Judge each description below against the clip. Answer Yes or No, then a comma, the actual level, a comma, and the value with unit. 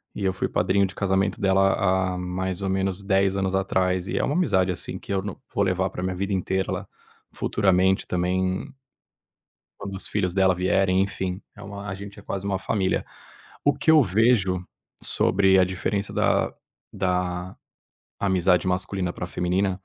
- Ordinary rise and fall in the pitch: No, narrow, 1.2 semitones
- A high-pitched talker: No, very low, 95 Hz